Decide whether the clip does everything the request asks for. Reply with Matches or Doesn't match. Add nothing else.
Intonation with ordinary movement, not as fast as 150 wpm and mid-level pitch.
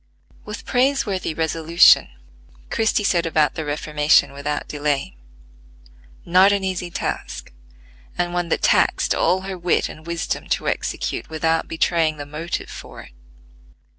Matches